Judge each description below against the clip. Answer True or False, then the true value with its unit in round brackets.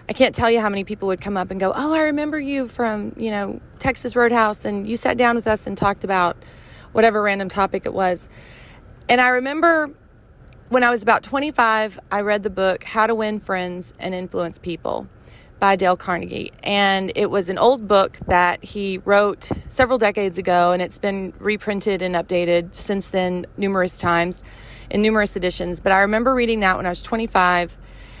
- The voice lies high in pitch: True (200 Hz)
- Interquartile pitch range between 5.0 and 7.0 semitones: False (3.8 semitones)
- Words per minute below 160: False (195 wpm)